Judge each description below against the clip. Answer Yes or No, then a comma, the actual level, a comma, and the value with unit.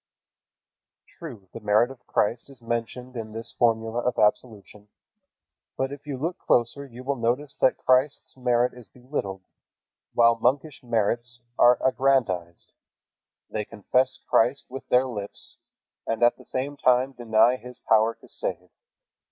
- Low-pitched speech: Yes, low, 120 Hz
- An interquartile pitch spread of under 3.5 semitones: Yes, narrow, 2.5 semitones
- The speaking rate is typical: Yes, average, 145 wpm